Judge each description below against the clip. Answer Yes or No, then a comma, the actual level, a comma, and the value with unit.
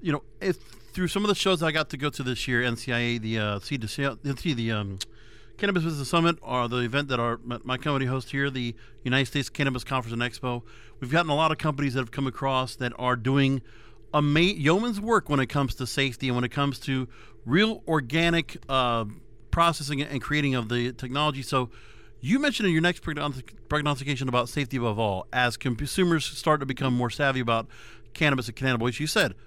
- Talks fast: Yes, fast, 210 wpm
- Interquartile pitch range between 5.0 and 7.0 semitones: No, average, 3.8 semitones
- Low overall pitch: Yes, low, 130 Hz